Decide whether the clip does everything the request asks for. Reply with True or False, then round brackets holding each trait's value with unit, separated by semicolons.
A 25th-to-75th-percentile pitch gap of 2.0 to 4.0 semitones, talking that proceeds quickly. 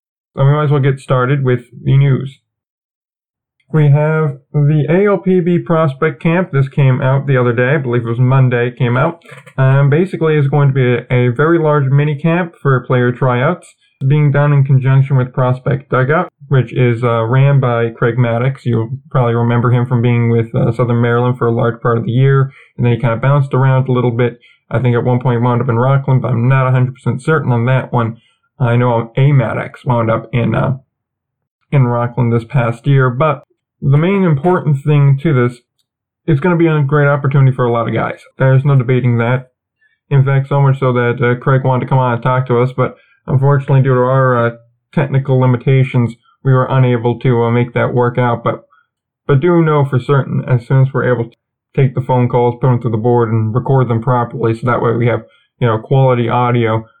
True (2.7 semitones; 220 wpm)